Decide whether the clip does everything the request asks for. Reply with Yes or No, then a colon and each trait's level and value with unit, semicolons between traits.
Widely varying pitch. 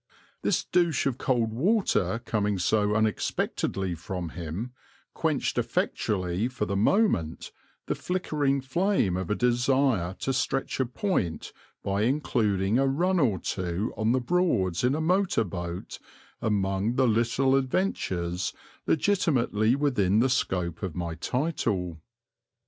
Yes: wide, 6.4 semitones